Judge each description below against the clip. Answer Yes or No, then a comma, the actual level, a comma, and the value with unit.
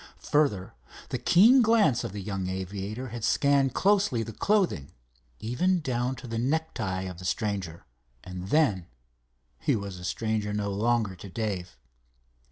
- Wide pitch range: Yes, wide, 6.0 semitones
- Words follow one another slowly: No, average, 145 wpm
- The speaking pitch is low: Yes, low, 105 Hz